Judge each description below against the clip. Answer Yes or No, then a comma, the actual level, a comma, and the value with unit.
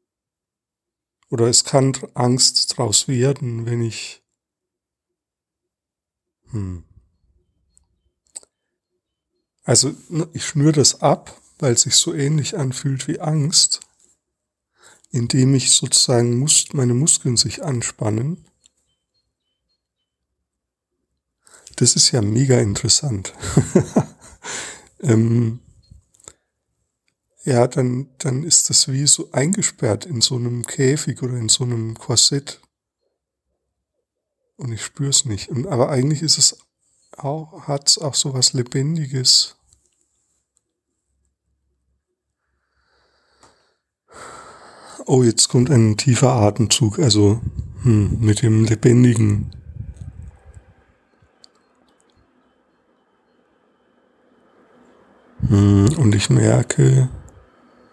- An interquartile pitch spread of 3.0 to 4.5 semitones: No, average, 4.9 semitones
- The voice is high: No, low, 125 Hz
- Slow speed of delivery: Yes, slow, 85 wpm